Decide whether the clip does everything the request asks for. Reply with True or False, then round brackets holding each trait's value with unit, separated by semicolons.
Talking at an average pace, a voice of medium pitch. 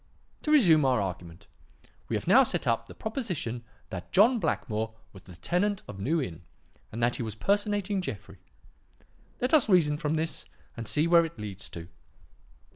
True (175 wpm; 150 Hz)